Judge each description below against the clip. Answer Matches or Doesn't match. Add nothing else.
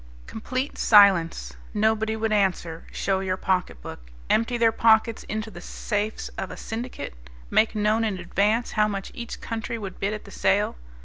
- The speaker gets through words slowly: Doesn't match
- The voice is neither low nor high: Doesn't match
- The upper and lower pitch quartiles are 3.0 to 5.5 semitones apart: Doesn't match